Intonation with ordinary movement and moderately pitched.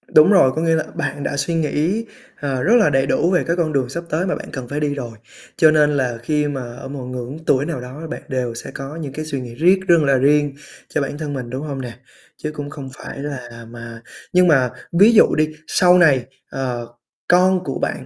Yes: average, 3.8 semitones; medium, 145 Hz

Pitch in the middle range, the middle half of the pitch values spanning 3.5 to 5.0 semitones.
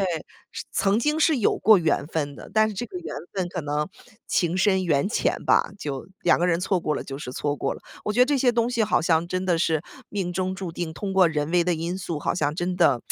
Yes: medium, 180 Hz; average, 4.1 semitones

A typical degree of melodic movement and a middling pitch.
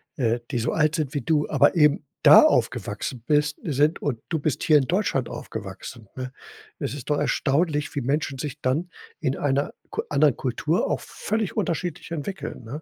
Yes: average, 3.5 semitones; medium, 145 Hz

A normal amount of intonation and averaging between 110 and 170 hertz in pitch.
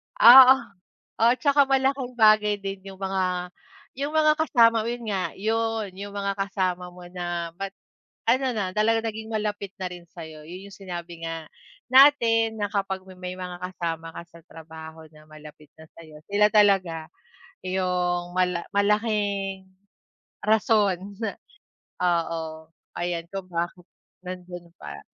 No: average, 3.7 semitones; high, 190 Hz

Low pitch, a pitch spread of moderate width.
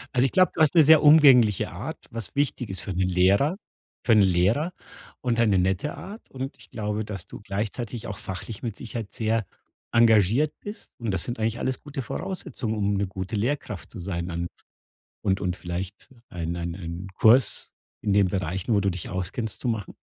Yes: low, 105 Hz; average, 4.7 semitones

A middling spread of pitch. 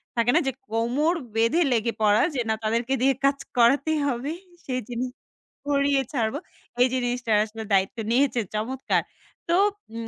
Yes: average, 3.3 semitones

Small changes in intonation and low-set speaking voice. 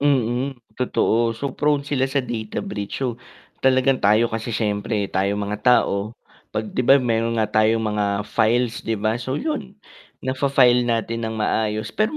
No: average, 3.3 semitones; low, 115 Hz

